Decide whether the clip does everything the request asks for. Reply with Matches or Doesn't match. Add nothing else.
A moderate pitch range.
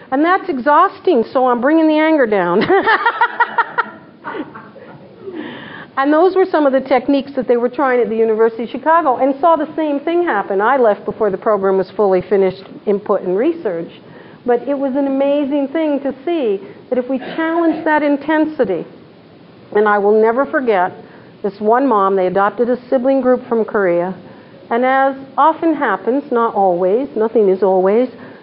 Doesn't match